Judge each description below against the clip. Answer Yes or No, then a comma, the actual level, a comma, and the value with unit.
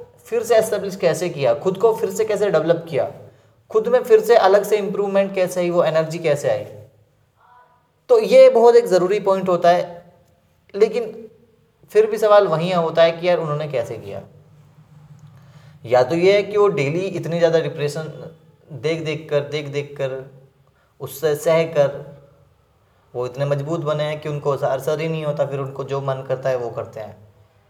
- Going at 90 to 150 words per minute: No, average, 180 wpm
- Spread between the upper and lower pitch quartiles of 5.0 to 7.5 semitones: Yes, wide, 5.4 semitones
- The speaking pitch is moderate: Yes, medium, 160 Hz